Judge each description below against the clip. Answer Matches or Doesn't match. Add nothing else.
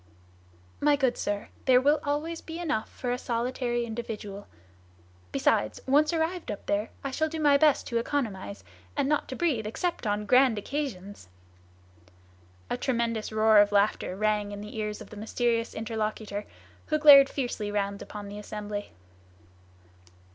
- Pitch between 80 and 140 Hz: Doesn't match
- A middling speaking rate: Matches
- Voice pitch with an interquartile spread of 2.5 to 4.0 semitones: Doesn't match